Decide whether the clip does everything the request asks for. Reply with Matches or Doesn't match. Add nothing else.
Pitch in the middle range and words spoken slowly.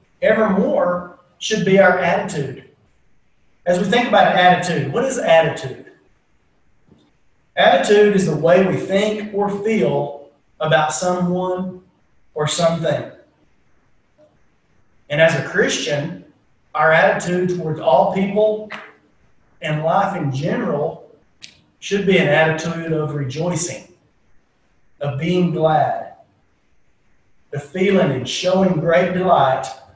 Matches